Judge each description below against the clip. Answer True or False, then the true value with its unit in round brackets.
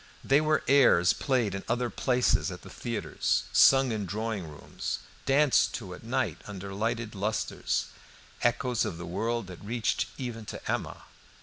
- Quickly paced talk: False (160 wpm)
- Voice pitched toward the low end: True (115 Hz)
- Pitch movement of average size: True (4.0 semitones)